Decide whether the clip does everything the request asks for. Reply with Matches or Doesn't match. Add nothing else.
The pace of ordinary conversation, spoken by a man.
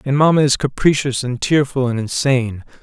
Matches